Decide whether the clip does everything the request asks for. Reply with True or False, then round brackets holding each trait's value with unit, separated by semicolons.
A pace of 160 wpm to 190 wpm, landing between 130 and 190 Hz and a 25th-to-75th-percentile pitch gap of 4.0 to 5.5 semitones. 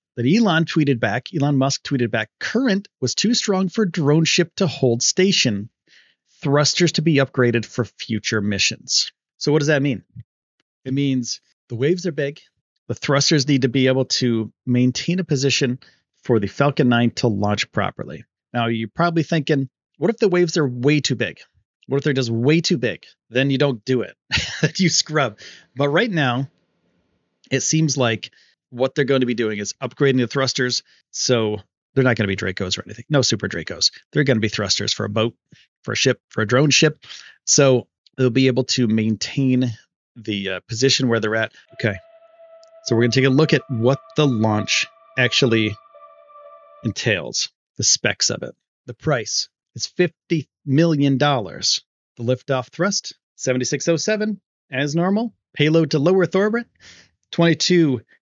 True (175 wpm; 135 Hz; 5.2 semitones)